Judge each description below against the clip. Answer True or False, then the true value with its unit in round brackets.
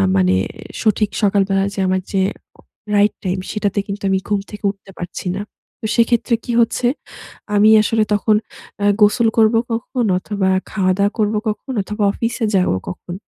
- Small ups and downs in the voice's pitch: True (2.2 semitones)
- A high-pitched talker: True (205 Hz)